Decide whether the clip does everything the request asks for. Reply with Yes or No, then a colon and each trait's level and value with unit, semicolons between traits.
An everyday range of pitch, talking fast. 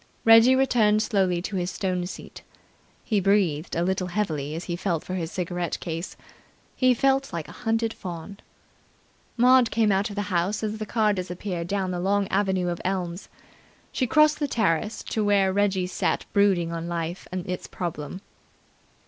No: average, 3.3 semitones; average, 175 wpm